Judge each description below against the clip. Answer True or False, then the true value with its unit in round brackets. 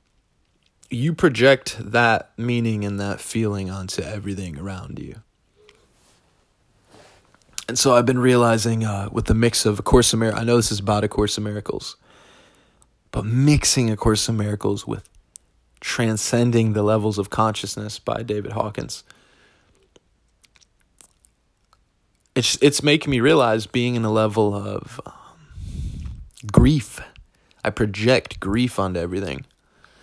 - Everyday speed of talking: False (130 wpm)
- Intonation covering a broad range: False (3.0 semitones)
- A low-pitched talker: True (110 Hz)